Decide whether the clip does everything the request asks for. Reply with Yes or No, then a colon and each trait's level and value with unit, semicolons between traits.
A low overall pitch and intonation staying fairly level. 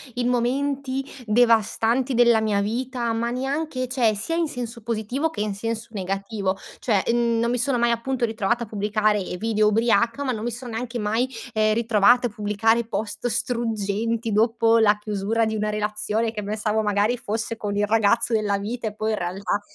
No: high, 225 Hz; narrow, 2.3 semitones